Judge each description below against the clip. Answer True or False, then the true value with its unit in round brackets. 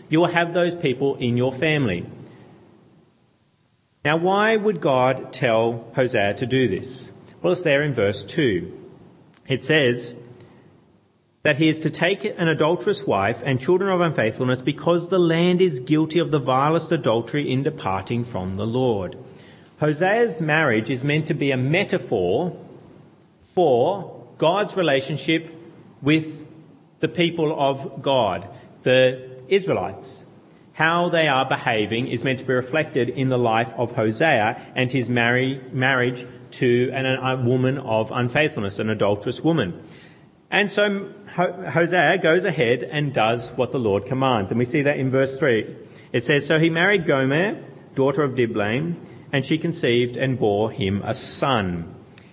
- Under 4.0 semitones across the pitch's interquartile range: False (5.0 semitones)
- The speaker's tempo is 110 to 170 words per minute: True (150 wpm)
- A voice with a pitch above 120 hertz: True (140 Hz)